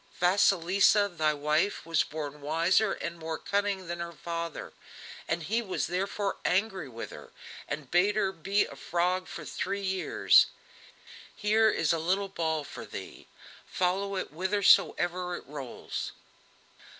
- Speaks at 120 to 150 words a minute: Yes, average, 140 wpm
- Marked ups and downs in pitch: No, average, 3.4 semitones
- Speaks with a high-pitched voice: No, medium, 180 Hz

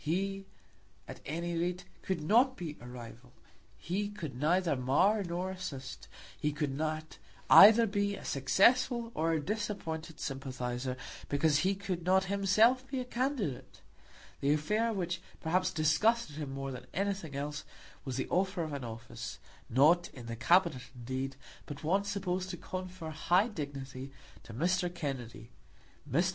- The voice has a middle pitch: Yes, medium, 165 Hz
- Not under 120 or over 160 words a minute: Yes, average, 150 wpm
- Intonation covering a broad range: Yes, wide, 5.9 semitones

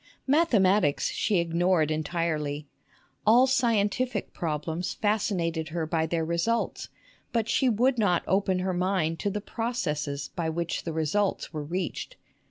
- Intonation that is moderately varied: Yes, average, 4.7 semitones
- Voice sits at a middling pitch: Yes, medium, 180 Hz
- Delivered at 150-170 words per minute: No, slow, 135 wpm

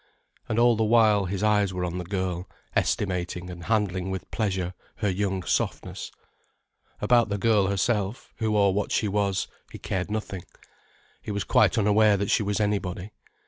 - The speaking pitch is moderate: No, low, 100 Hz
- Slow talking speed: No, average, 170 wpm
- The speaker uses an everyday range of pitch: No, narrow, 2.3 semitones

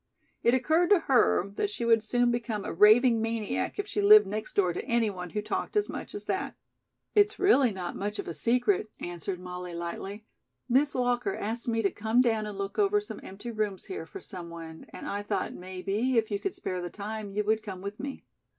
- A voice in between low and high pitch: No, high, 220 Hz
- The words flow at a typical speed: No, fast, 215 wpm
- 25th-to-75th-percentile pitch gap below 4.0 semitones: No, average, 4.3 semitones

